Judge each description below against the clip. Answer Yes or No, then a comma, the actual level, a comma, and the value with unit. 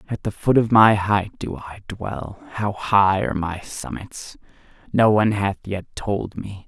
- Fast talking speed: No, average, 180 wpm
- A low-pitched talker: Yes, low, 100 Hz